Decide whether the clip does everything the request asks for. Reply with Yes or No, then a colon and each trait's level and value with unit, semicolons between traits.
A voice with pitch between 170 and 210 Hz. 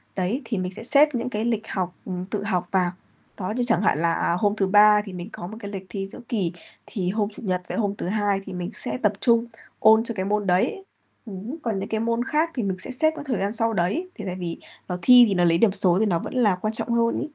Yes: high, 205 Hz